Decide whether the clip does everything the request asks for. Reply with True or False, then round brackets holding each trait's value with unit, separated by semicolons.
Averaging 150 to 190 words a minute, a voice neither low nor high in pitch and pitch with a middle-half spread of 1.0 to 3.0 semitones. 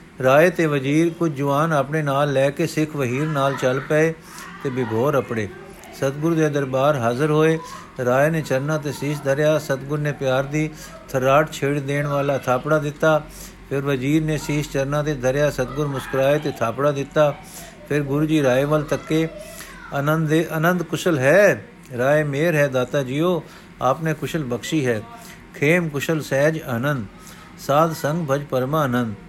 True (160 wpm; 150 Hz; 2.5 semitones)